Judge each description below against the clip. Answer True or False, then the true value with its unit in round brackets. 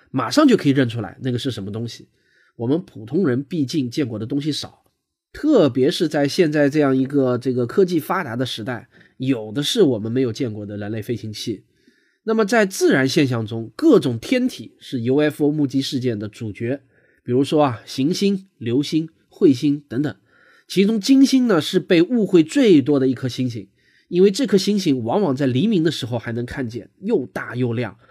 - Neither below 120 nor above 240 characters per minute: False (290 characters per minute)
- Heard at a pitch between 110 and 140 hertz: True (135 Hz)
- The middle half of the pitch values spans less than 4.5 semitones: False (5.3 semitones)